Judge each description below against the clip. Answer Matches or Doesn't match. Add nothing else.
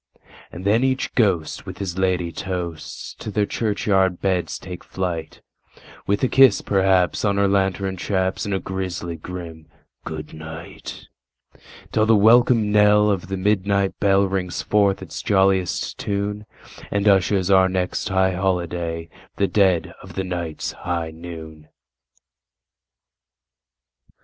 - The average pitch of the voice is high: Doesn't match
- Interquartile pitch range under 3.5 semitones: Matches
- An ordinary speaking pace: Doesn't match